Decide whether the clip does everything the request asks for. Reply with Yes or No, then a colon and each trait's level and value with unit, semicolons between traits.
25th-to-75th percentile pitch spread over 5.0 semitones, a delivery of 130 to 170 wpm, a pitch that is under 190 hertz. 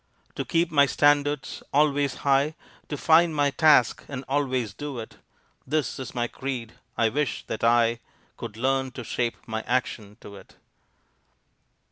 No: average, 3.5 semitones; average, 150 wpm; low, 135 Hz